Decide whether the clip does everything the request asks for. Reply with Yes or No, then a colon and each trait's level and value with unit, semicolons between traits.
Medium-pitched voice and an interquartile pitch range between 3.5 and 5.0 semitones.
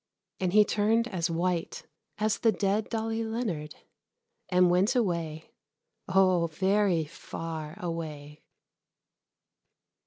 Yes: medium, 180 Hz; average, 4.3 semitones